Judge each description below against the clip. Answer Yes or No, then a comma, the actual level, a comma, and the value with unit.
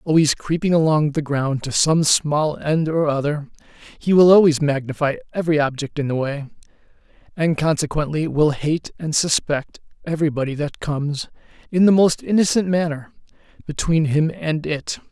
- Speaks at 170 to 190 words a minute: No, average, 150 wpm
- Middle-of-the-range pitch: Yes, medium, 155 Hz